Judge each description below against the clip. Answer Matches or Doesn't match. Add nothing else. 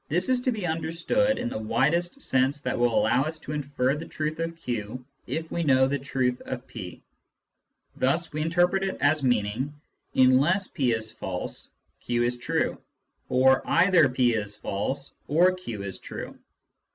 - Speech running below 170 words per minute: Doesn't match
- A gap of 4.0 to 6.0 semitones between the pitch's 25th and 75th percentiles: Matches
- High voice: Doesn't match